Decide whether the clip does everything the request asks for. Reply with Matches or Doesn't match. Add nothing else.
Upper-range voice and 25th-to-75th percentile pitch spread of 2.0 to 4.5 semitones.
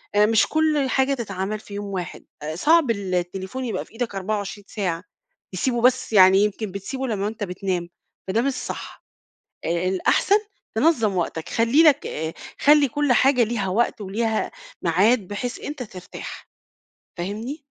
Doesn't match